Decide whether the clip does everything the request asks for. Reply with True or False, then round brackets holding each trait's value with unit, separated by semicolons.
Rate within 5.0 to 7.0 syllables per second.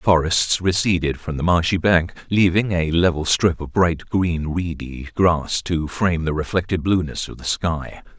False (4.5 syllables/s)